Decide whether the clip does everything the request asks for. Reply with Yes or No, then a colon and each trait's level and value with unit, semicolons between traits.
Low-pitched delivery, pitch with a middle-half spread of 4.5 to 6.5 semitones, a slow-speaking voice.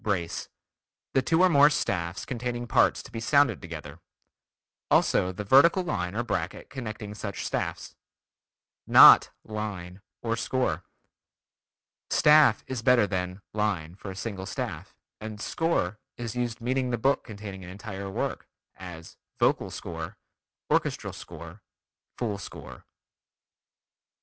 Yes: low, 105 Hz; average, 4.8 semitones; slow, 130 wpm